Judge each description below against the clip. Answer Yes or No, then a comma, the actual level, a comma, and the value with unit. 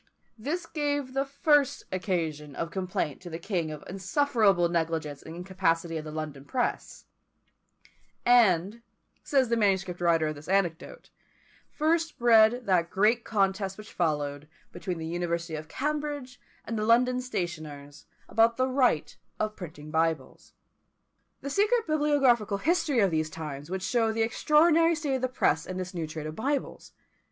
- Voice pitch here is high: Yes, high, 195 Hz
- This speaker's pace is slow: No, average, 155 wpm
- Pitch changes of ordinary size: No, wide, 7.7 semitones